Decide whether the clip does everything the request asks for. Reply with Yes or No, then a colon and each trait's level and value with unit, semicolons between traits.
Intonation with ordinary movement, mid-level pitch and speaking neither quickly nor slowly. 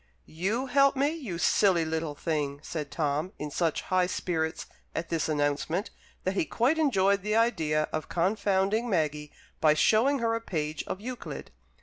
No: wide, 6.1 semitones; medium, 180 Hz; average, 160 wpm